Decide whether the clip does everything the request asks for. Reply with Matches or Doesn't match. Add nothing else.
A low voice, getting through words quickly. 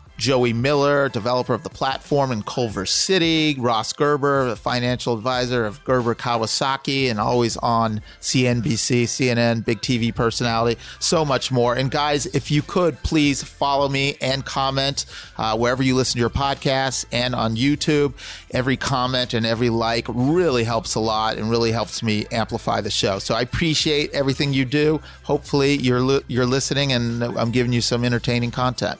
Doesn't match